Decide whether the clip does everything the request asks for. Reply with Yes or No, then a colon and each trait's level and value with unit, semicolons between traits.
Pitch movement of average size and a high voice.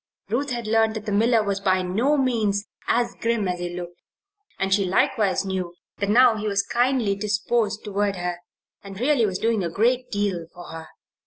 Yes: average, 3.4 semitones; high, 205 Hz